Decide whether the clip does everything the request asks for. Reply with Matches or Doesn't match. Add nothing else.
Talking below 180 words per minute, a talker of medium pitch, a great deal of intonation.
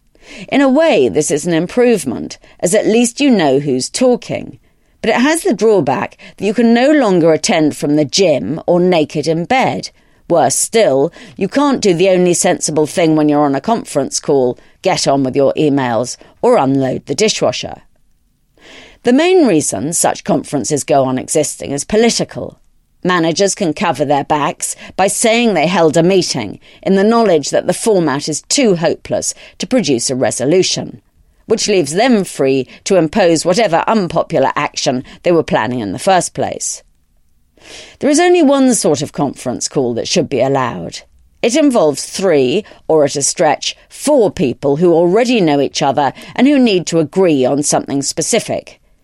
Matches